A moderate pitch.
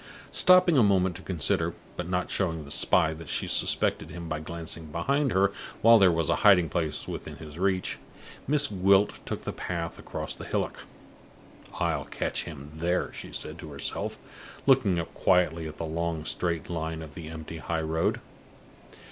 No: very low, 85 Hz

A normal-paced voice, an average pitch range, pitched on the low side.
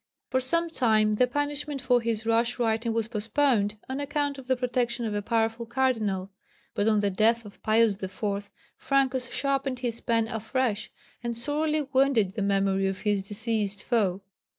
No: average, 170 wpm; average, 3.8 semitones; high, 230 Hz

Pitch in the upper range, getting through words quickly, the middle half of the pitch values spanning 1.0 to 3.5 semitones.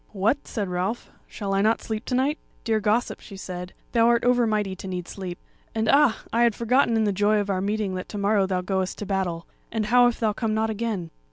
Yes: high, 210 Hz; fast, 240 wpm; average, 3.2 semitones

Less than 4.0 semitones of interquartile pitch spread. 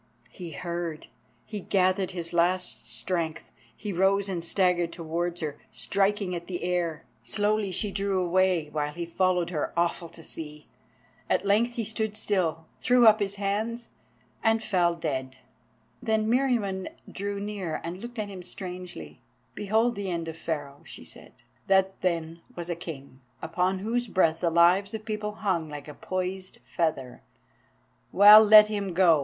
Yes: average, 3.4 semitones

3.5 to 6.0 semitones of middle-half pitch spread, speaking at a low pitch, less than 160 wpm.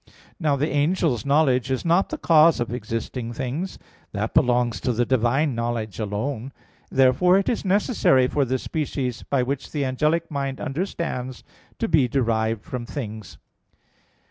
Yes: average, 4.2 semitones; low, 130 Hz; average, 150 wpm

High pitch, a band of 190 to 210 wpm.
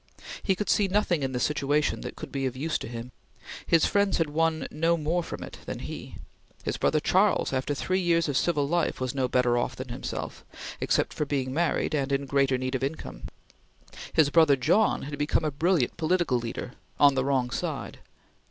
No: medium, 145 Hz; average, 200 wpm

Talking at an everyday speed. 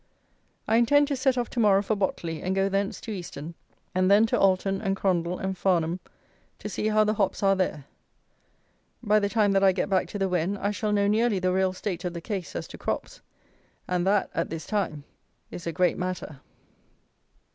No: fast, 210 wpm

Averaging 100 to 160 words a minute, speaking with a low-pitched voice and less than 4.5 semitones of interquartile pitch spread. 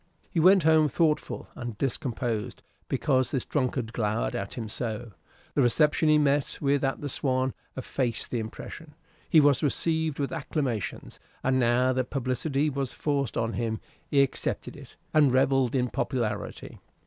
Yes: average, 155 wpm; low, 130 Hz; average, 3.5 semitones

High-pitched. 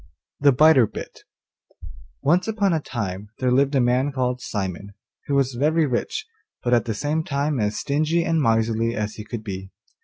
No: low, 125 Hz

